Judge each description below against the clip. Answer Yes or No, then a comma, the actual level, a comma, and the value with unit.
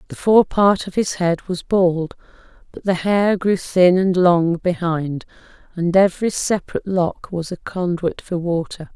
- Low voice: No, medium, 180 Hz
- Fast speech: No, average, 170 wpm